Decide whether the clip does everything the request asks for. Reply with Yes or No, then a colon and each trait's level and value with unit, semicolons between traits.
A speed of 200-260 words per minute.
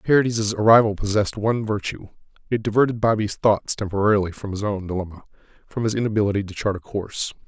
No: average, 170 wpm